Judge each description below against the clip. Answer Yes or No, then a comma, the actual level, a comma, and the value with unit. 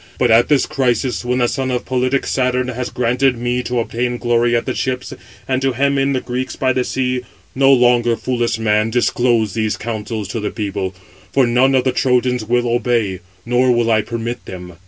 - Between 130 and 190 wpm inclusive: No, average, 200 wpm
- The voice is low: Yes, low, 125 Hz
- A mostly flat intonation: Yes, narrow, 1.6 semitones